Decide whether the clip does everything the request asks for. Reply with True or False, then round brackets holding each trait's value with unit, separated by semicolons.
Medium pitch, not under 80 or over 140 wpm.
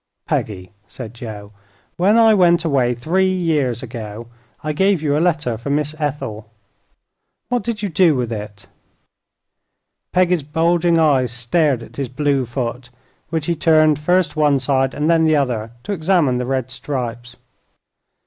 False (145 Hz; 155 wpm)